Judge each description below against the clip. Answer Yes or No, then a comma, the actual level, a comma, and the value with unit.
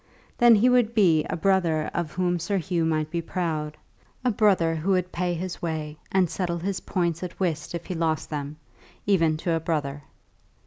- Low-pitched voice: No, medium, 170 Hz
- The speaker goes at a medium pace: Yes, average, 190 wpm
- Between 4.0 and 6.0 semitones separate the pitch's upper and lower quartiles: No, average, 2.9 semitones